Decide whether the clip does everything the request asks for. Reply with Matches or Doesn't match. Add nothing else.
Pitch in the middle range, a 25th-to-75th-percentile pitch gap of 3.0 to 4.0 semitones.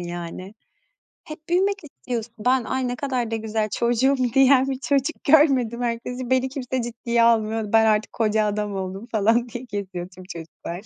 Doesn't match